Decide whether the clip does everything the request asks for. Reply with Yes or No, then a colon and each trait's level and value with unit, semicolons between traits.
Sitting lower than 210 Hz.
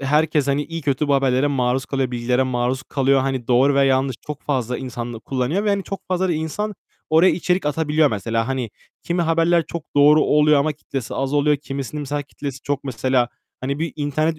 Yes: medium, 140 Hz